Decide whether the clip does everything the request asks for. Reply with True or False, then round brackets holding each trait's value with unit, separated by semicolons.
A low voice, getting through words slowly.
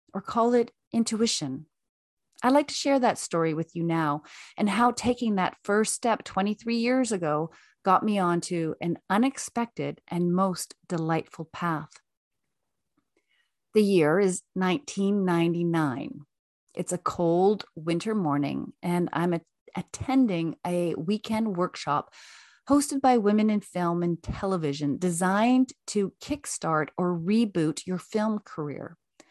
False (185 Hz; 125 wpm)